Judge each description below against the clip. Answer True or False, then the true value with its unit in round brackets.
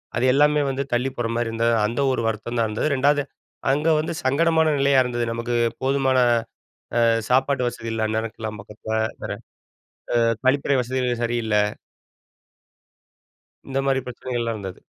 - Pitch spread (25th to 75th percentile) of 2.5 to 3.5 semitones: True (3.1 semitones)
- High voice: False (120 Hz)